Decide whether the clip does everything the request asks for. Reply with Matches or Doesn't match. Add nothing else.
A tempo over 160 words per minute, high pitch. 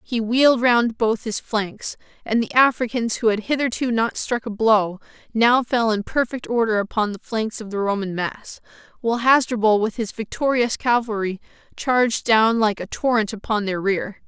Matches